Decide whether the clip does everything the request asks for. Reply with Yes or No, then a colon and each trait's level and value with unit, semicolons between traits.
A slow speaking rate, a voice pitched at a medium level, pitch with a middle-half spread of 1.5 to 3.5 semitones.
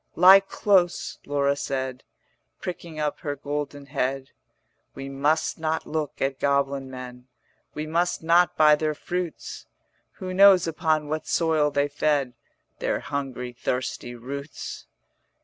Yes: slow, 130 wpm; medium, 145 Hz; average, 2.7 semitones